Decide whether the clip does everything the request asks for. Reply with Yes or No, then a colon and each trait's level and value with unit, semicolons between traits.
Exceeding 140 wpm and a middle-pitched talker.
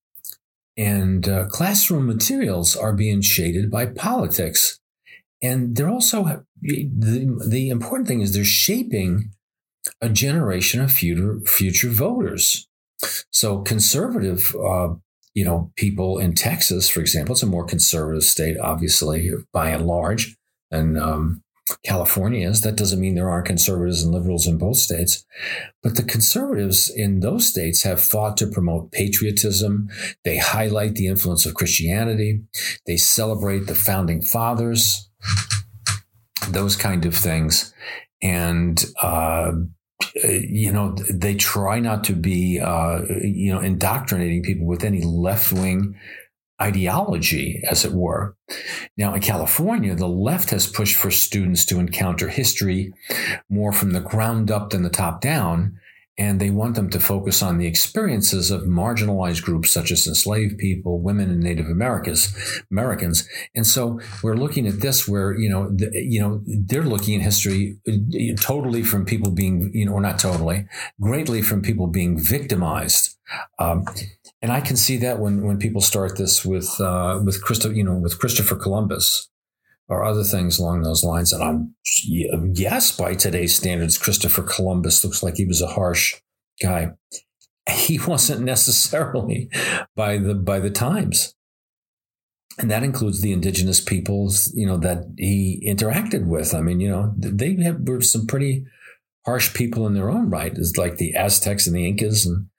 No: average, 155 wpm; low, 100 Hz